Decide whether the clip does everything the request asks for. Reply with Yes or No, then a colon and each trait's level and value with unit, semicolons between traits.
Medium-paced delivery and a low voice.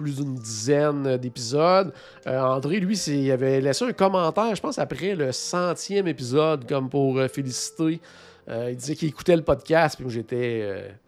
No: average, 185 wpm; medium, 145 Hz